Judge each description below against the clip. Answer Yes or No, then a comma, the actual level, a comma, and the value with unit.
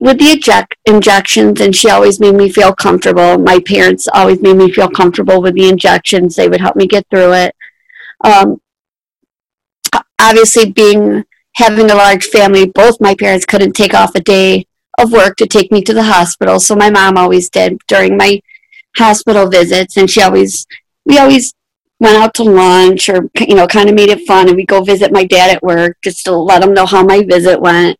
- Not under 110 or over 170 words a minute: No, average, 200 wpm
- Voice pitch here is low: No, high, 195 Hz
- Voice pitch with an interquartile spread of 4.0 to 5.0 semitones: No, narrow, 2.4 semitones